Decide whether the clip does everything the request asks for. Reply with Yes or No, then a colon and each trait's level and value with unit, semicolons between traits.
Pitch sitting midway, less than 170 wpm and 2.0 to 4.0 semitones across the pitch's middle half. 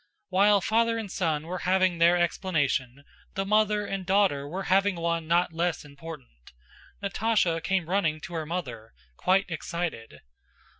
Yes: medium, 175 Hz; average, 145 wpm; average, 3.5 semitones